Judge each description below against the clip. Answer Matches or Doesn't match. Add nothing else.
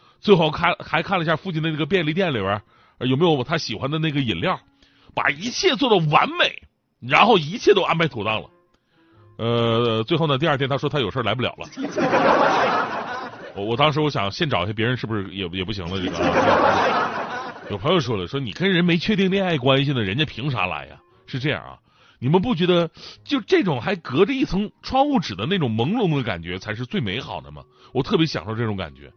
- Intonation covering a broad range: Matches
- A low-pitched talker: Doesn't match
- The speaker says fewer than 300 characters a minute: Doesn't match